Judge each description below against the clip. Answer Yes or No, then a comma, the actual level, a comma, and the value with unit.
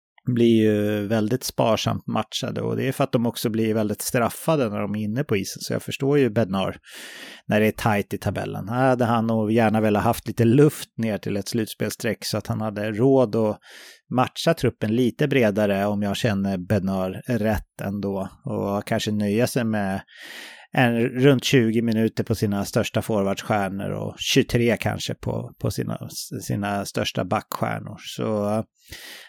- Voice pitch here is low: Yes, low, 110 Hz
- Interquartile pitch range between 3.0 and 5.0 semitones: No, narrow, 2.6 semitones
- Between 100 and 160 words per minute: No, average, 170 wpm